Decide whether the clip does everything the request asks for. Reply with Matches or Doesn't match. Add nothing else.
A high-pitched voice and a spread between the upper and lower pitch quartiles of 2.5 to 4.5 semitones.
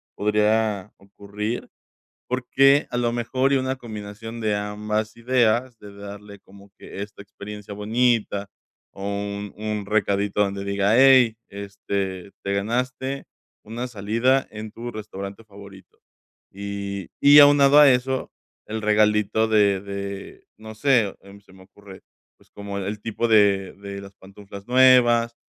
Doesn't match